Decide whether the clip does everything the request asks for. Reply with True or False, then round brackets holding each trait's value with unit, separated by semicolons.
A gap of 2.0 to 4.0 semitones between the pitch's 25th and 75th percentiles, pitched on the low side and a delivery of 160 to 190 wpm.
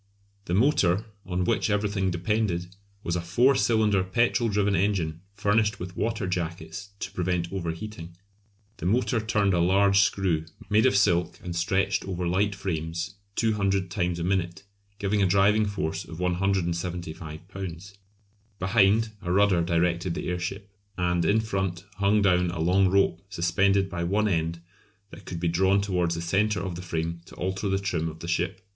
True (2.7 semitones; 95 Hz; 170 wpm)